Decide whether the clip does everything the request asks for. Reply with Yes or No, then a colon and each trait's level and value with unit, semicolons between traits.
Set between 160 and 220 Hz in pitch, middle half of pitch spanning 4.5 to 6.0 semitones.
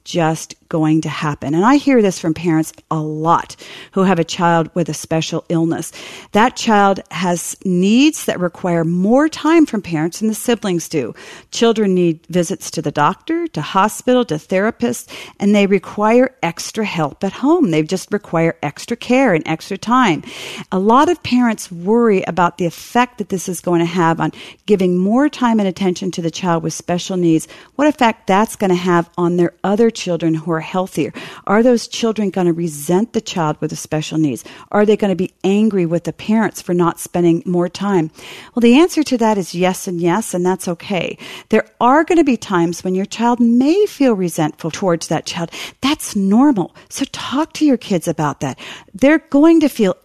Yes: medium, 185 Hz; average, 5.3 semitones